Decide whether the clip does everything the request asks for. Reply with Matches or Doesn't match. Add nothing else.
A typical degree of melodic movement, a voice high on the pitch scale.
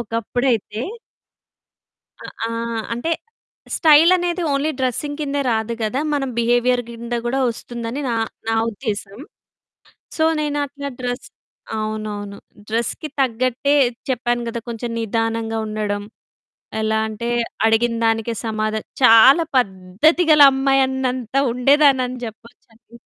Matches